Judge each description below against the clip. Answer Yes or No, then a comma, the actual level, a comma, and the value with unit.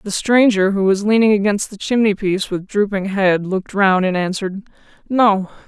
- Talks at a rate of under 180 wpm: Yes, average, 170 wpm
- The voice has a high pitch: Yes, high, 200 Hz